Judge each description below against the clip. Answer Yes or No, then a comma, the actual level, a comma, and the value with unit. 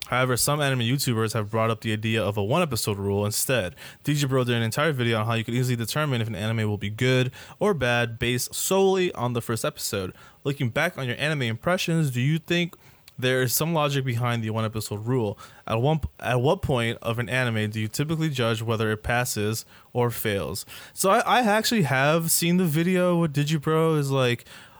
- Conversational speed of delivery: No, fast, 210 wpm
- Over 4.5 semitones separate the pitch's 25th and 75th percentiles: Yes, average, 5.0 semitones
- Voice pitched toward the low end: Yes, low, 125 Hz